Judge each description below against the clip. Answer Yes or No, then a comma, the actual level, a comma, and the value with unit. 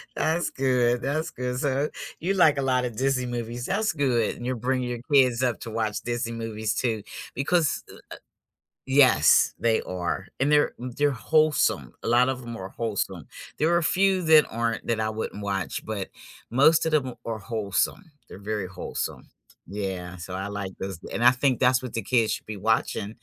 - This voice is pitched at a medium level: No, low, 120 Hz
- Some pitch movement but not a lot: Yes, average, 3.9 semitones